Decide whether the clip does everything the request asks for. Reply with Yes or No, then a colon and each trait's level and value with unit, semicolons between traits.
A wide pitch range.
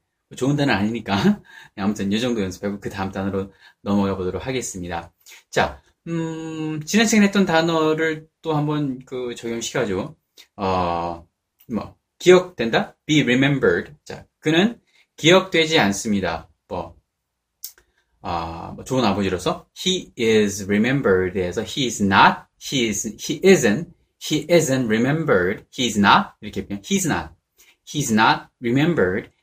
Yes: wide, 8.2 semitones